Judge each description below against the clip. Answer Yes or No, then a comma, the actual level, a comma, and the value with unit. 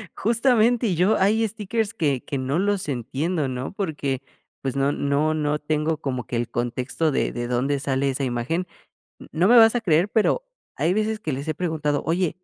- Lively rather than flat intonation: Yes, wide, 6.6 semitones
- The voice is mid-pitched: Yes, medium, 155 Hz